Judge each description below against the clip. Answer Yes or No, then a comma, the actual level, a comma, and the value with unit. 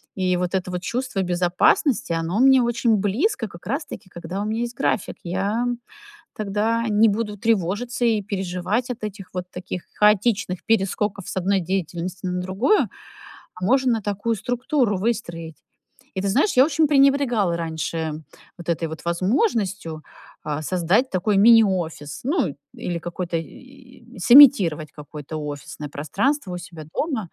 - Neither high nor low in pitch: No, high, 195 Hz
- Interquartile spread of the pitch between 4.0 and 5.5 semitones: Yes, average, 5.1 semitones